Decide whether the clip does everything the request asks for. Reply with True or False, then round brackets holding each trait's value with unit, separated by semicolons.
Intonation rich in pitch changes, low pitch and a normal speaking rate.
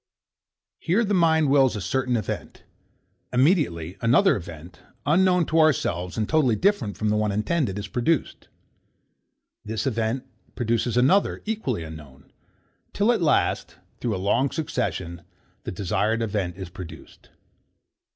False (8.0 semitones; 115 Hz; 130 wpm)